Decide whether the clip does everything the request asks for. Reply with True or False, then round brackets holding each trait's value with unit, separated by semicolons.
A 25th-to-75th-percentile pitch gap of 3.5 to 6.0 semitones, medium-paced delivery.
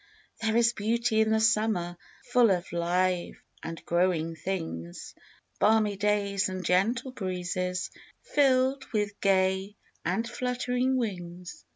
False (3.9 semitones; 115 wpm)